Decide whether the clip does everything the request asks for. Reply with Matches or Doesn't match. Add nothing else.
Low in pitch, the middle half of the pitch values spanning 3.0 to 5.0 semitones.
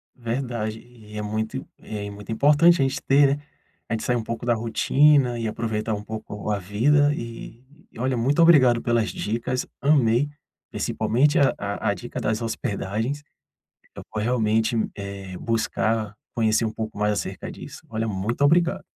Matches